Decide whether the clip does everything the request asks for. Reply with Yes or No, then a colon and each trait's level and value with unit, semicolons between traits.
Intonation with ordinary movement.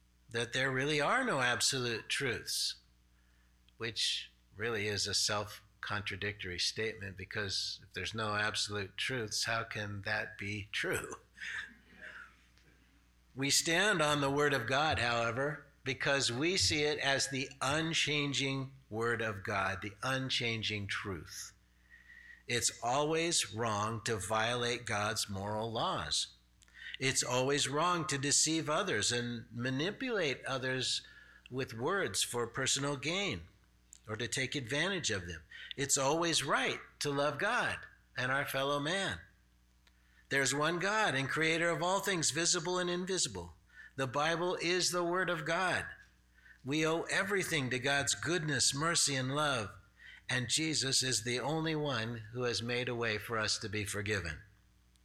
No: wide, 6.0 semitones